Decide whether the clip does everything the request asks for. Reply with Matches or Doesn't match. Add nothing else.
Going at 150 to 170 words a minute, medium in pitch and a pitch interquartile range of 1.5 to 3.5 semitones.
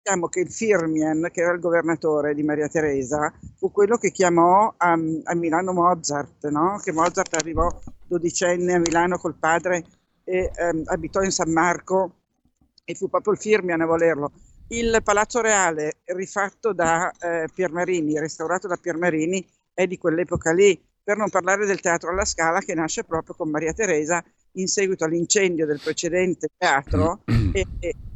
Matches